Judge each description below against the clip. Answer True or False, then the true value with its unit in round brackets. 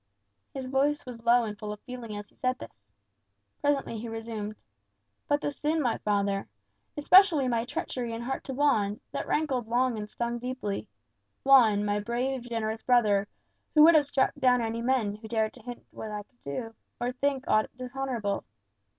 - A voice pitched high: True (240 Hz)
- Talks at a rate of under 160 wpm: False (180 wpm)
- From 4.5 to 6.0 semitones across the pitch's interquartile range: False (3.6 semitones)